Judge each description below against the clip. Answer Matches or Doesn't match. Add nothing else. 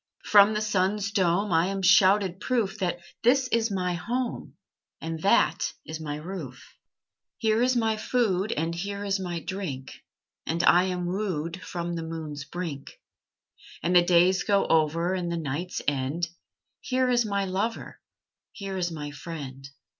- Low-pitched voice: Doesn't match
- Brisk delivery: Doesn't match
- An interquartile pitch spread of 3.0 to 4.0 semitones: Matches